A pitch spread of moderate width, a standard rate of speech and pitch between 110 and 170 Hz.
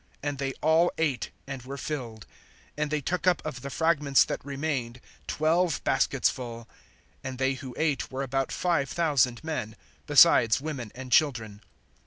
Yes: average, 3.5 semitones; average, 160 wpm; low, 135 Hz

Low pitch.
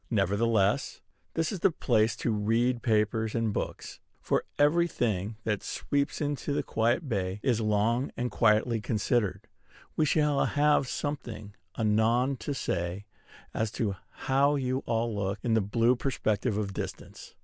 Yes: low, 115 Hz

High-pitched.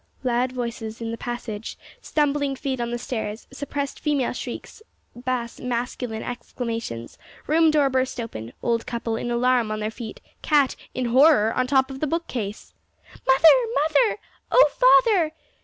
Yes: very high, 250 Hz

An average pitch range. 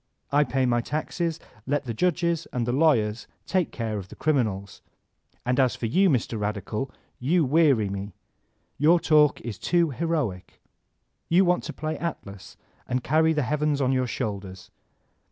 No: wide, 6.1 semitones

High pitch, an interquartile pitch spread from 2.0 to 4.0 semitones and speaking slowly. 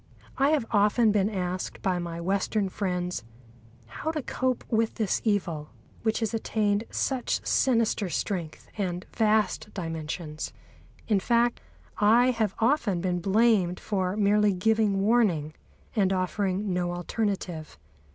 Yes: high, 200 Hz; average, 3.7 semitones; slow, 130 wpm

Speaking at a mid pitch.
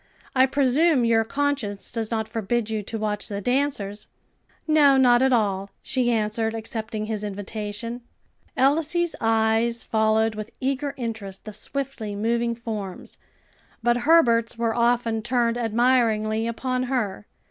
No: high, 230 Hz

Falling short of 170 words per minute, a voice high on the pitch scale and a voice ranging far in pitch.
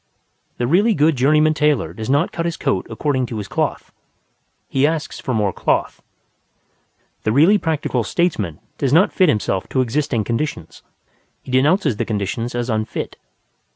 No: average, 155 wpm; low, 130 Hz; wide, 5.8 semitones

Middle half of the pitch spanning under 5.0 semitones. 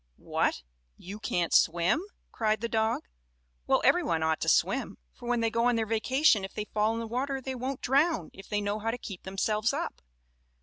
Yes: average, 3.2 semitones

